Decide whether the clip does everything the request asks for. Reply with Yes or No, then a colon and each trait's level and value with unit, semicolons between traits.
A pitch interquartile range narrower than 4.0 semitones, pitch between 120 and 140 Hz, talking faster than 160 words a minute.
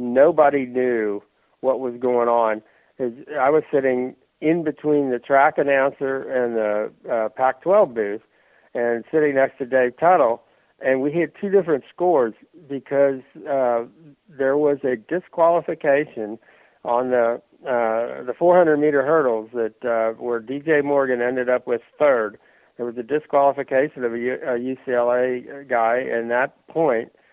No: average, 3.0 semitones; low, 130 Hz; average, 140 wpm